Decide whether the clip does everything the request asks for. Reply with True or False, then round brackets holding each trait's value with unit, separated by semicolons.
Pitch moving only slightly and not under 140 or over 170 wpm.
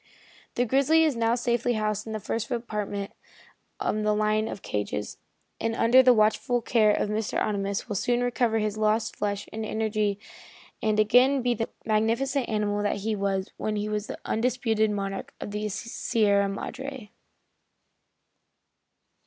True (2.2 semitones; 155 wpm)